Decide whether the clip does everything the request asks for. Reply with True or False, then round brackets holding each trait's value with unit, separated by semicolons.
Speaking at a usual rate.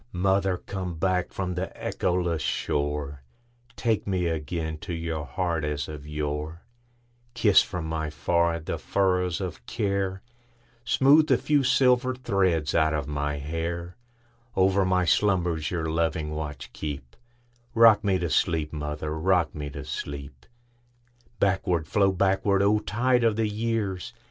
False (125 wpm)